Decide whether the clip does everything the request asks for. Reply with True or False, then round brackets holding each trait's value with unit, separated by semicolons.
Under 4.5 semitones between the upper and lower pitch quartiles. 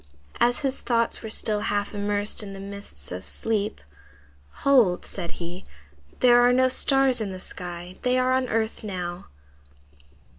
False (4.9 semitones)